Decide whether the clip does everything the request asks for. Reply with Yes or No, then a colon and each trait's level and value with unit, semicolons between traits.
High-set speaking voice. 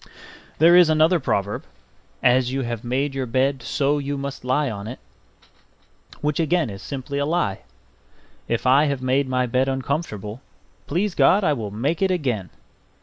No: low, 135 Hz